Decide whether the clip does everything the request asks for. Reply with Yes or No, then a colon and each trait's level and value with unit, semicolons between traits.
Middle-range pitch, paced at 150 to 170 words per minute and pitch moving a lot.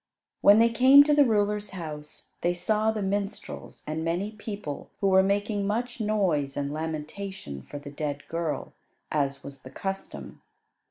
No: high, 195 Hz; average, 160 wpm; wide, 5.7 semitones